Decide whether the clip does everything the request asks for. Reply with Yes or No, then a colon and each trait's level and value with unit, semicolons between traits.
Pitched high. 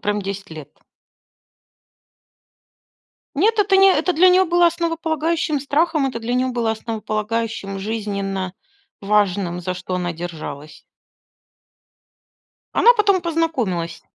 Yes: high, 225 Hz